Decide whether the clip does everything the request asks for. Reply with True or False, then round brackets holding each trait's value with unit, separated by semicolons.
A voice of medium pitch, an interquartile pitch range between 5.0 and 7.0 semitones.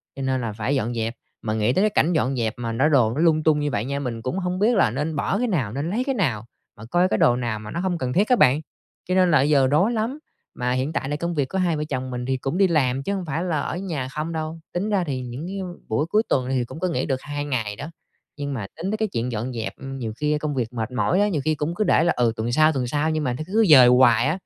True (145 Hz; 5.5 semitones)